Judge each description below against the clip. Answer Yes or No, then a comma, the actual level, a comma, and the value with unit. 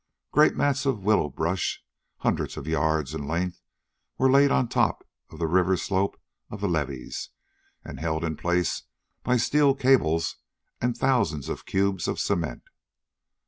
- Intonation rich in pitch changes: Yes, wide, 7.4 semitones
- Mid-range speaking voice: No, very low, 90 Hz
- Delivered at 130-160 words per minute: Yes, average, 150 wpm